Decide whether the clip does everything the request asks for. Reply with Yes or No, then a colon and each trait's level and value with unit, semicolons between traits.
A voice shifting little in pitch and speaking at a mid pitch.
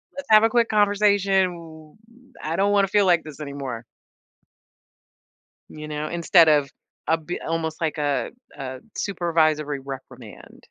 No: average, 4.6 semitones; medium, 160 Hz